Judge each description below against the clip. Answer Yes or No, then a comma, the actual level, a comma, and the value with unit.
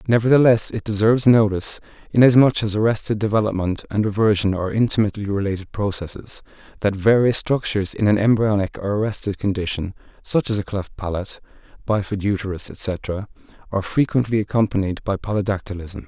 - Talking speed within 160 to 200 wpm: No, slow, 135 wpm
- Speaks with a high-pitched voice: No, low, 105 Hz